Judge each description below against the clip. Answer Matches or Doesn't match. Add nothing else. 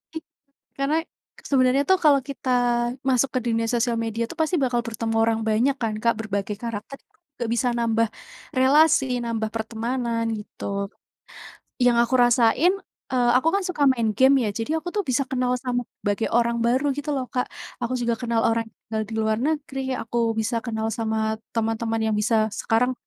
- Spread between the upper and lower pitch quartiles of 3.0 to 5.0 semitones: Doesn't match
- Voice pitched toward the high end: Matches